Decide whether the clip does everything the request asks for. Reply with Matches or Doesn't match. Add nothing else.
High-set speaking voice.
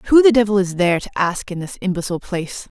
Matches